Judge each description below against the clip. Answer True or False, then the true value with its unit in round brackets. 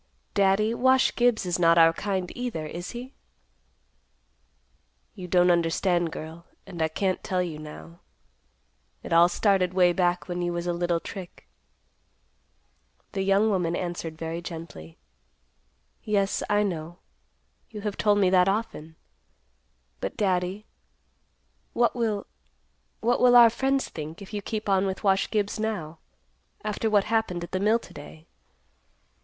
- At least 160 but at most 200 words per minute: False (145 wpm)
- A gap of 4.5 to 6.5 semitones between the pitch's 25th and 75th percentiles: False (3.6 semitones)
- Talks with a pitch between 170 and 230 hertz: True (185 Hz)